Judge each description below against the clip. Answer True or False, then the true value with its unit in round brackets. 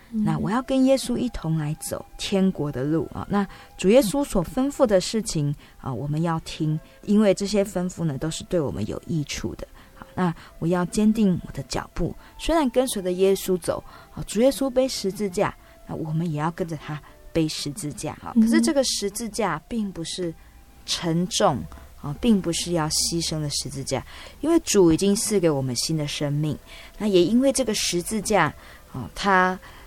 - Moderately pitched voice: True (175 Hz)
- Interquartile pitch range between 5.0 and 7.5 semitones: True (5.4 semitones)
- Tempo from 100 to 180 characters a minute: False (265 characters per minute)